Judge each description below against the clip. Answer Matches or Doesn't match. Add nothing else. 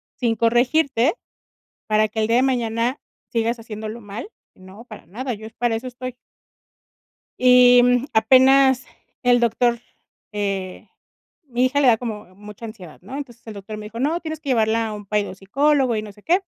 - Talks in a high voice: Matches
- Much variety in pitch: Doesn't match